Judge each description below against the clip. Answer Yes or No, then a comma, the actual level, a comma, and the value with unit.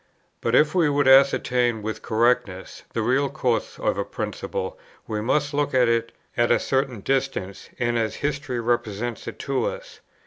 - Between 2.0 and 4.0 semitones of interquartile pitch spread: Yes, average, 3.3 semitones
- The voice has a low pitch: Yes, low, 125 Hz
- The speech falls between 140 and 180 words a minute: Yes, average, 170 wpm